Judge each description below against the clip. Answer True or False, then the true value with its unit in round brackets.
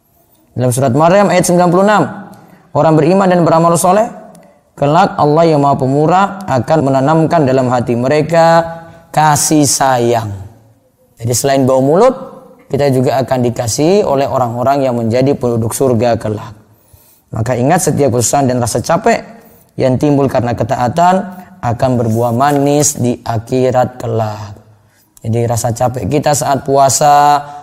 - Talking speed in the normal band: True (130 wpm)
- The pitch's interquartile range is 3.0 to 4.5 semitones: False (5.1 semitones)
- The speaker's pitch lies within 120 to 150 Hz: True (135 Hz)